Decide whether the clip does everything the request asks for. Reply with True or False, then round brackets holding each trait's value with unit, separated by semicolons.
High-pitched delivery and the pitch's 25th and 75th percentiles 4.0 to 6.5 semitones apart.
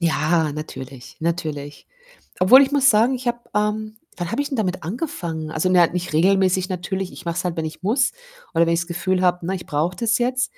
False (180 Hz; 4.6 semitones)